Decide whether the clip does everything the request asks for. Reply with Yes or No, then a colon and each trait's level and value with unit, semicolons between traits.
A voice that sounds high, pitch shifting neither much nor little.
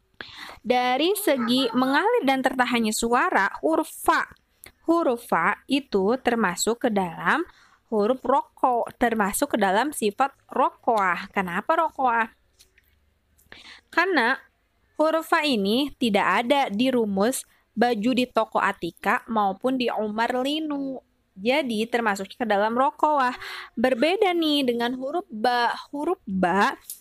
Yes: very high, 250 Hz; average, 4.6 semitones